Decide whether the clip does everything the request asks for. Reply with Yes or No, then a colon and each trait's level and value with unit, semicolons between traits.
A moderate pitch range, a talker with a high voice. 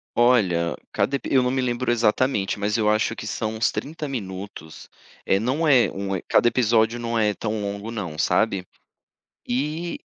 No: average, 3.9 semitones; low, 115 Hz